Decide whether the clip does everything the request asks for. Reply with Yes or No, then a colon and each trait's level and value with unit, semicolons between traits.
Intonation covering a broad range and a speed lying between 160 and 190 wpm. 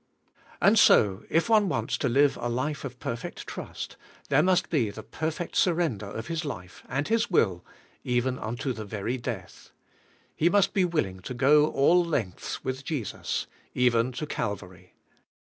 Yes: wide, 6.3 semitones; average, 165 wpm